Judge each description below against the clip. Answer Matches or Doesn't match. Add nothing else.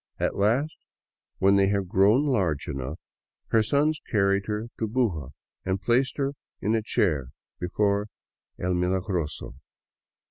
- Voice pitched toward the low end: Matches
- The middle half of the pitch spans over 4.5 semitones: Doesn't match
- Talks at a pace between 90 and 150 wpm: Matches